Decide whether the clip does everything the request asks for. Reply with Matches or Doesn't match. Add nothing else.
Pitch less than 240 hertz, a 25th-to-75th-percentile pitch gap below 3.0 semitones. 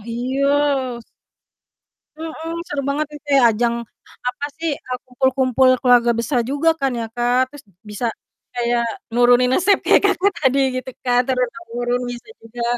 Doesn't match